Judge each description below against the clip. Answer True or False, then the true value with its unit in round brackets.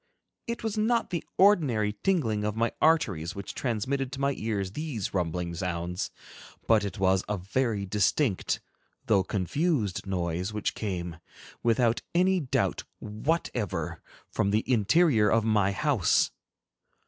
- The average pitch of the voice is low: True (110 Hz)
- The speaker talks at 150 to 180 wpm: False (135 wpm)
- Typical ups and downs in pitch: False (6.4 semitones)